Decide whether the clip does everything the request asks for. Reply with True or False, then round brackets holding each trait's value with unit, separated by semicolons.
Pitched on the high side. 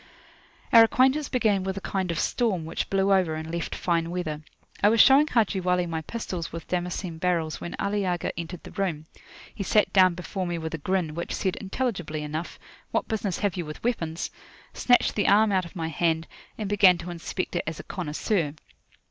False (180 Hz)